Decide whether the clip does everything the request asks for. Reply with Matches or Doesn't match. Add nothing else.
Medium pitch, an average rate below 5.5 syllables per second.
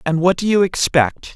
Matches